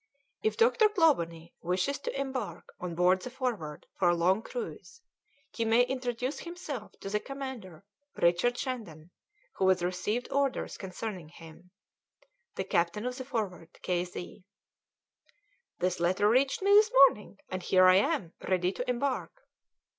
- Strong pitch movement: Yes, wide, 6.8 semitones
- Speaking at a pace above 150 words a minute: No, average, 145 wpm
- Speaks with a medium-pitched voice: No, high, 210 Hz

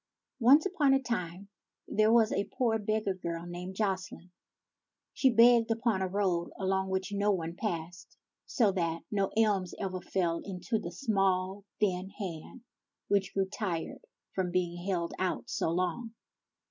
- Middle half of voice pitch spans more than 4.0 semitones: No, average, 3.2 semitones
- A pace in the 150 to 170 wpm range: Yes, average, 160 wpm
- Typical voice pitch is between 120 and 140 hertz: No, high, 190 Hz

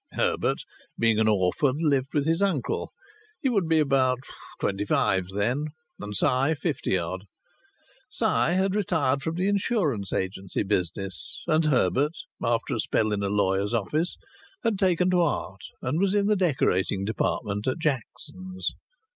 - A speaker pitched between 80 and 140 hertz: Yes, low, 135 Hz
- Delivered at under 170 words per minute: Yes, average, 150 wpm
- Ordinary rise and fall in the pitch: No, wide, 8.8 semitones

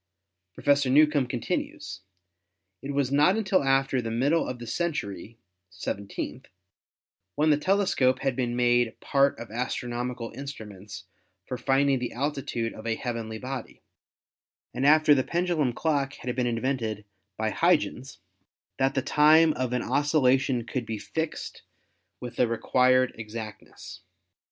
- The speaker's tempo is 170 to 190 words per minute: No, slow, 135 wpm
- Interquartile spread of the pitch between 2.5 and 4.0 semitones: Yes, average, 3.4 semitones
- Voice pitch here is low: Yes, low, 130 Hz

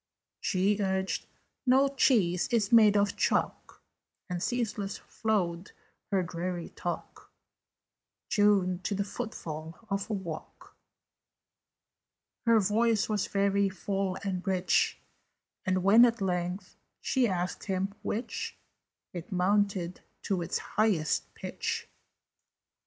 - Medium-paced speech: No, slow, 110 wpm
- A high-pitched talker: Yes, high, 195 Hz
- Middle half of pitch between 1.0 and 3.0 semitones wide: Yes, average, 2.7 semitones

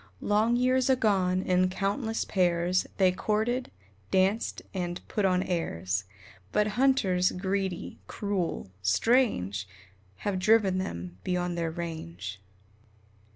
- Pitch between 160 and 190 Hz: Yes, medium, 185 Hz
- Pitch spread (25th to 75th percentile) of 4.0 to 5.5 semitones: No, average, 3.6 semitones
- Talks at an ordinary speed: No, slow, 110 wpm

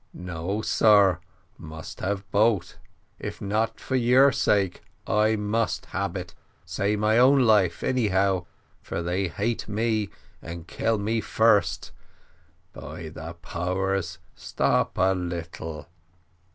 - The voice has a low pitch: Yes, low, 100 Hz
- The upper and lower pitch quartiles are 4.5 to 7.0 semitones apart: No, average, 3.9 semitones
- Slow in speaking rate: Yes, slow, 120 wpm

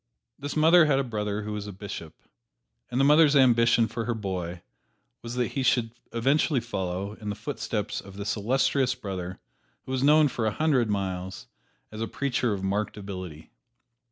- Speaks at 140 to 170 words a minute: No, average, 180 wpm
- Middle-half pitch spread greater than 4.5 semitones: Yes, average, 5.0 semitones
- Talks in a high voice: No, low, 115 Hz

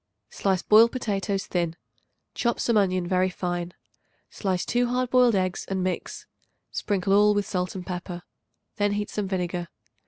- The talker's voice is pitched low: No, high, 195 Hz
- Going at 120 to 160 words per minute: Yes, average, 155 wpm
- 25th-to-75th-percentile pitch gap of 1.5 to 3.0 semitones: Yes, narrow, 2.5 semitones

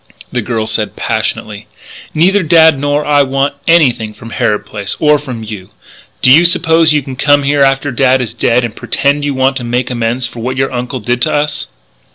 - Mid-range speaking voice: No, low, 130 Hz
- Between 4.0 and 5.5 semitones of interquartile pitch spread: No, average, 3.6 semitones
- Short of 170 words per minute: No, fast, 205 wpm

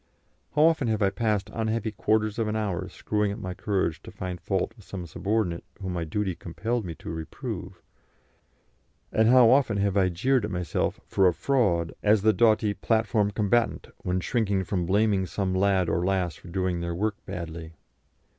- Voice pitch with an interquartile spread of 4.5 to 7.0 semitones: No, average, 3.4 semitones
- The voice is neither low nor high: No, low, 100 Hz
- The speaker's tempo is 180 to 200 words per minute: Yes, average, 185 wpm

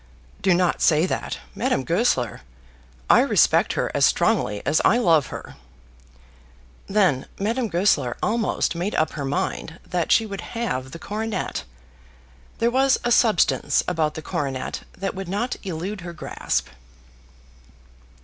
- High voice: No, medium, 180 Hz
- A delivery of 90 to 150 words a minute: Yes, average, 140 wpm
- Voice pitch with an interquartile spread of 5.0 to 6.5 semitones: Yes, wide, 5.5 semitones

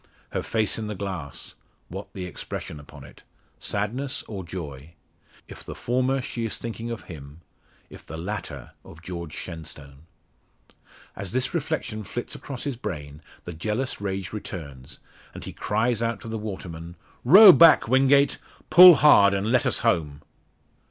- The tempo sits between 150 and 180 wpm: Yes, average, 155 wpm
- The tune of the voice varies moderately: No, wide, 6.6 semitones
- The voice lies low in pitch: Yes, low, 105 Hz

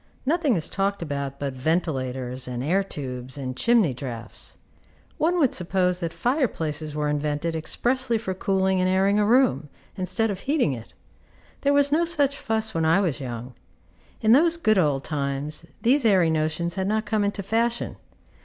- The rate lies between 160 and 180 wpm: Yes, average, 170 wpm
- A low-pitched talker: No, medium, 185 Hz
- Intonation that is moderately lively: No, wide, 7.4 semitones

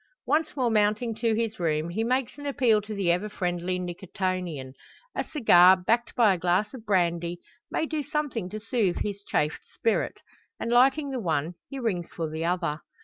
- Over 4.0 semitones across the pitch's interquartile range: Yes, average, 5.2 semitones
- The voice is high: Yes, high, 205 Hz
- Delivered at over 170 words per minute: Yes, average, 185 wpm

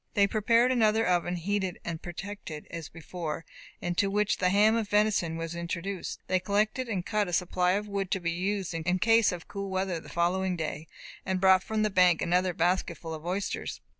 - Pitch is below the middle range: No, medium, 185 Hz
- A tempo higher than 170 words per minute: Yes, average, 195 wpm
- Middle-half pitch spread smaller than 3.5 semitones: Yes, average, 3.0 semitones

